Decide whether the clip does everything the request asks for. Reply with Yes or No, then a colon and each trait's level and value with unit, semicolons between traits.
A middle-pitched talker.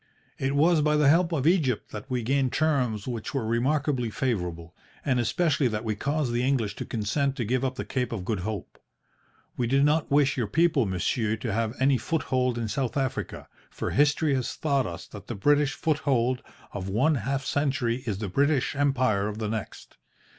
No: low, 130 Hz